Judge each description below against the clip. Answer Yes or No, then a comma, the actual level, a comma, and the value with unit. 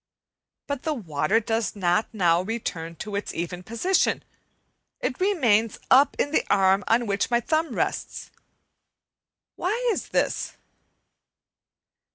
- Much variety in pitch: Yes, wide, 7.1 semitones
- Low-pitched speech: No, high, 225 Hz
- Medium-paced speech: No, slow, 125 wpm